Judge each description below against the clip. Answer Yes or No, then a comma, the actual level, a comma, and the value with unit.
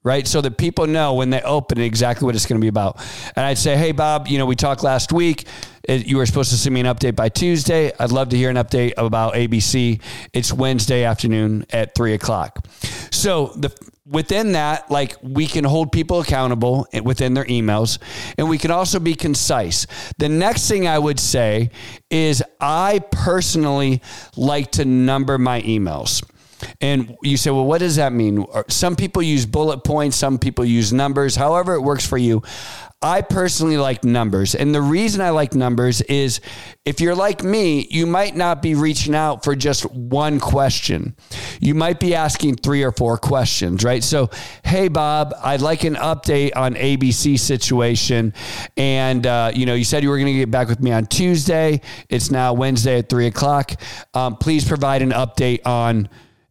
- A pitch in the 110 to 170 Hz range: Yes, low, 135 Hz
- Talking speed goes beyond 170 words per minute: Yes, average, 190 wpm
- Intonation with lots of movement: No, average, 3.9 semitones